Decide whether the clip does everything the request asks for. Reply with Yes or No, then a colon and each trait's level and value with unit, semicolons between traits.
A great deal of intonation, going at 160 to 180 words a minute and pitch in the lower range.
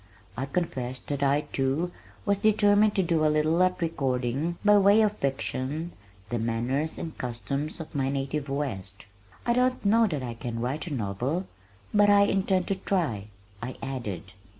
No: wide, 6.5 semitones; average, 170 wpm; medium, 150 Hz